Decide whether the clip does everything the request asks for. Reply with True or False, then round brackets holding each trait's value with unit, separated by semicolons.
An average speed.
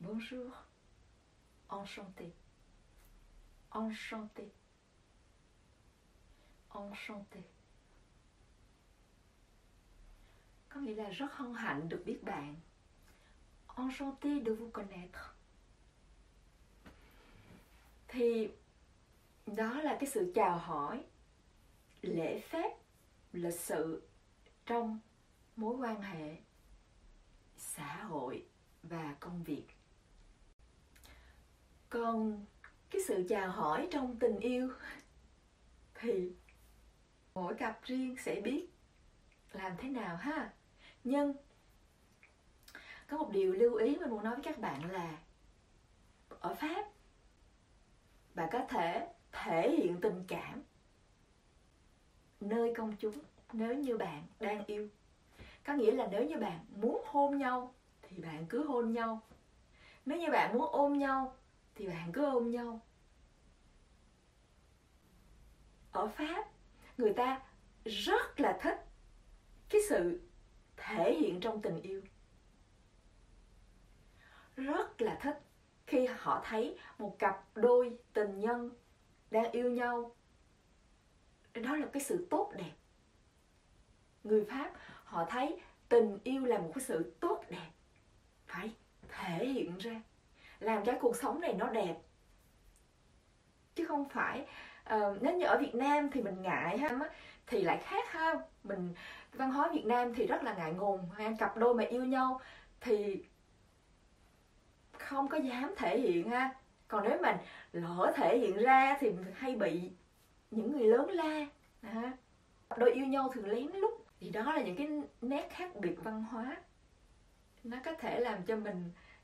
False (125 wpm)